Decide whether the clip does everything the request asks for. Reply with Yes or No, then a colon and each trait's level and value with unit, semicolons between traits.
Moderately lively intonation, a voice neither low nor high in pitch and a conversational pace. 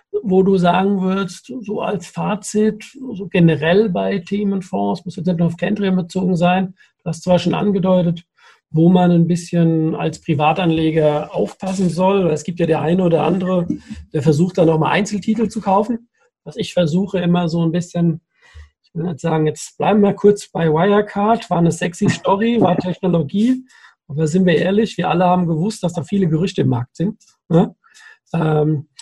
Yes: average, 3.3 semitones; medium, 180 Hz; average, 180 wpm